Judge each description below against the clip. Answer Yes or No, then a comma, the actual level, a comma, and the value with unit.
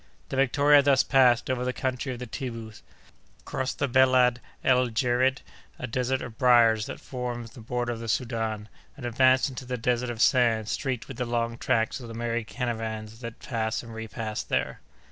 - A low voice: Yes, low, 120 Hz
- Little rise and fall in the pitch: Yes, narrow, 2.1 semitones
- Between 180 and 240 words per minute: Yes, average, 185 wpm